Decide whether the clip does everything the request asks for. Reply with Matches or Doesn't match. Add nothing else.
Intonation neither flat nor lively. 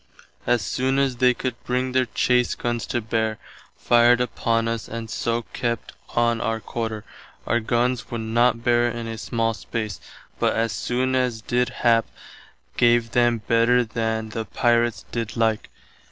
Doesn't match